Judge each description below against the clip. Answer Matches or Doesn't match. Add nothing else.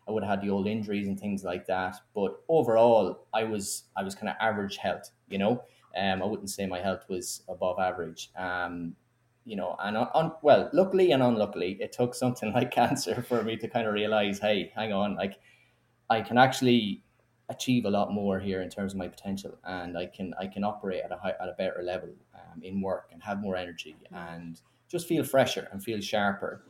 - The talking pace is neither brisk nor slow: Doesn't match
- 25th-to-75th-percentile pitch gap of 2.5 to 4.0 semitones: Matches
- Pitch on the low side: Matches